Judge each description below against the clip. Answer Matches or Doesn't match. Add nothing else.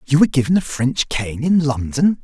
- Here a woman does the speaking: Doesn't match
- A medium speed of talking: Doesn't match